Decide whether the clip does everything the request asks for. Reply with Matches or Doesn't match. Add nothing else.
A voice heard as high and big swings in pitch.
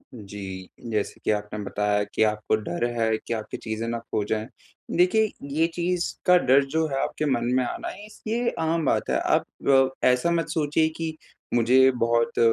Doesn't match